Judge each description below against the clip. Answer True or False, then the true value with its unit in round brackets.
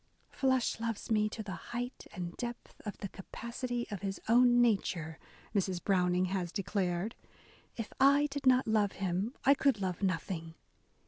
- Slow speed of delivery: False (165 wpm)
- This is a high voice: True (210 Hz)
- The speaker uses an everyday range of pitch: True (4.6 semitones)